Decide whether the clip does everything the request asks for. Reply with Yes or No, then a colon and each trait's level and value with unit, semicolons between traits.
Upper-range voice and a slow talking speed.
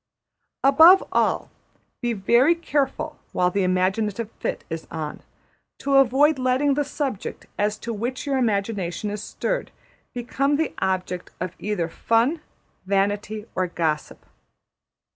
Yes: high, 225 Hz; slow, 125 wpm